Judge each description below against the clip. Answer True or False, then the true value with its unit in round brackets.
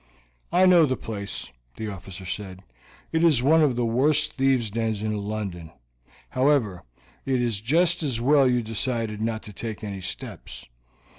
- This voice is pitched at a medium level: False (115 Hz)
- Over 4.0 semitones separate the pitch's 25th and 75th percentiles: True (4.6 semitones)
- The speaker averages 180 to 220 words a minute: False (160 wpm)